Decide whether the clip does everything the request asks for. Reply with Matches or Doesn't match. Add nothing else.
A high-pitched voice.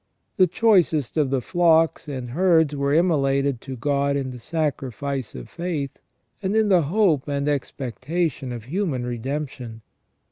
Doesn't match